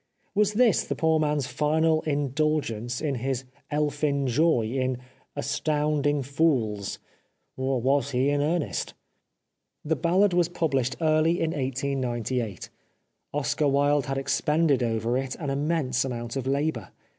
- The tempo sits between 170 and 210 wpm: No, slow, 135 wpm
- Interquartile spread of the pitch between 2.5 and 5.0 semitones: Yes, average, 3.2 semitones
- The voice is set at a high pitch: No, medium, 140 Hz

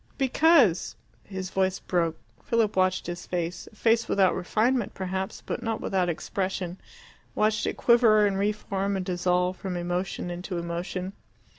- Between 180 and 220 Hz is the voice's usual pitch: Yes, high, 190 Hz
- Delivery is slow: No, average, 155 wpm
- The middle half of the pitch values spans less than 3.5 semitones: Yes, average, 2.9 semitones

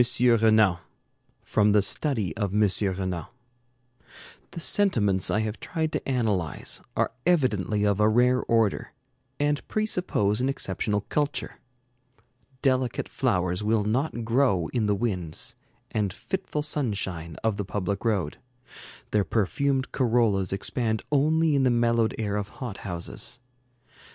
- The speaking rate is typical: No, slow, 130 wpm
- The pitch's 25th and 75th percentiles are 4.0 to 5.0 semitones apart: Yes, average, 4.5 semitones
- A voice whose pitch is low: Yes, low, 110 Hz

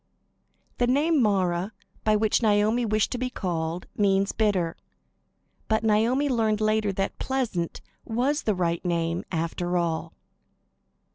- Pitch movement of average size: Yes, average, 4.4 semitones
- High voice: Yes, high, 210 Hz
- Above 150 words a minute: No, slow, 135 wpm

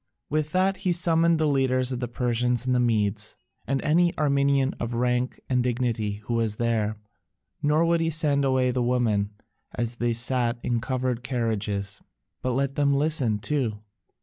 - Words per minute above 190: No, average, 170 wpm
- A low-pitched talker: Yes, low, 125 Hz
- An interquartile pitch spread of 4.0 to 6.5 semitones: No, average, 3.2 semitones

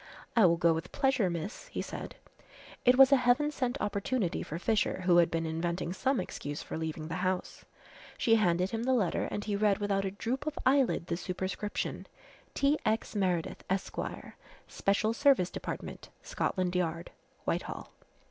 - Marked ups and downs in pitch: Yes, wide, 5.9 semitones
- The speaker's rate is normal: Yes, average, 165 wpm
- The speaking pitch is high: Yes, high, 195 Hz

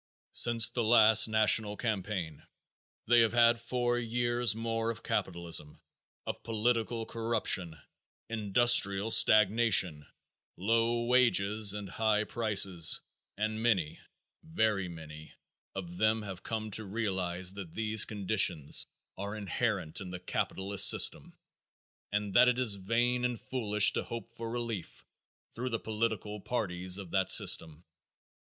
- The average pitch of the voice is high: No, low, 110 Hz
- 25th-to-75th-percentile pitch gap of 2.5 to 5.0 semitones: Yes, average, 3.3 semitones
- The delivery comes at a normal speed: No, slow, 125 wpm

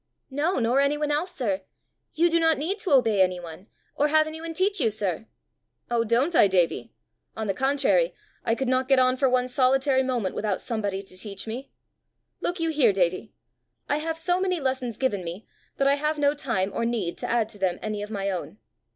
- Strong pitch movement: Yes, wide, 6.3 semitones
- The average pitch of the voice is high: Yes, very high, 255 Hz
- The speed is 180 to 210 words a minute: Yes, fast, 205 wpm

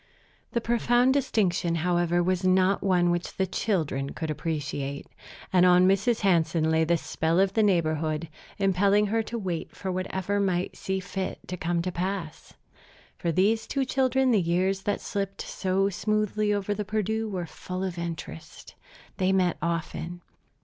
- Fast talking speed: No, average, 160 wpm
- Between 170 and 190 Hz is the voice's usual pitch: Yes, medium, 185 Hz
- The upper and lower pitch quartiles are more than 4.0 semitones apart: No, average, 3.0 semitones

